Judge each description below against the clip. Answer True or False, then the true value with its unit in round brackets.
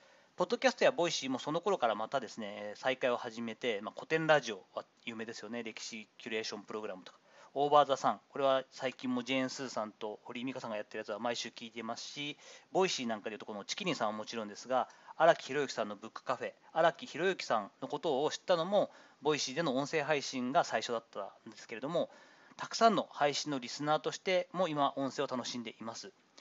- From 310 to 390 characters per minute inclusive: False (475 characters per minute)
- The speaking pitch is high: False (135 Hz)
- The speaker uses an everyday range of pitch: False (6.0 semitones)